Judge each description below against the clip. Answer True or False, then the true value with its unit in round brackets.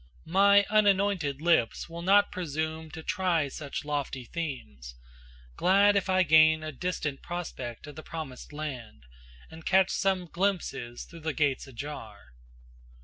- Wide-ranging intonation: False (4.8 semitones)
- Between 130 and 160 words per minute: True (140 wpm)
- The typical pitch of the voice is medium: True (160 Hz)